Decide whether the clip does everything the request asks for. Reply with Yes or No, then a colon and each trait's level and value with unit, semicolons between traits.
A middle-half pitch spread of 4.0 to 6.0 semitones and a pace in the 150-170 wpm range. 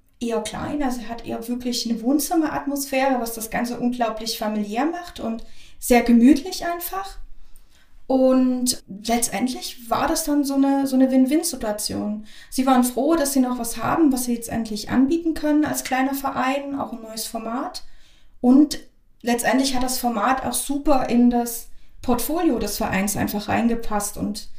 No: average, 3.2 semitones; average, 155 wpm